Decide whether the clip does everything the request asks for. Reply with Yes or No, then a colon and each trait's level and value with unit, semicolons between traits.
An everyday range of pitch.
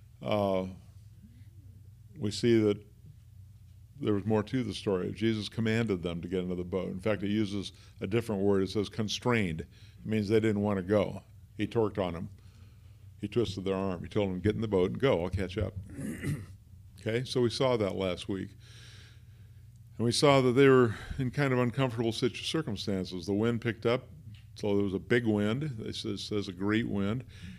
No: narrow, 2.3 semitones